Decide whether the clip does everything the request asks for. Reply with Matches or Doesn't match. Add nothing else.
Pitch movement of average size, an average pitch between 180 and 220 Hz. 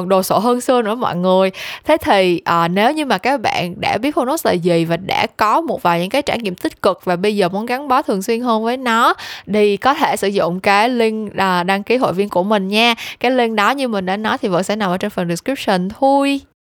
Matches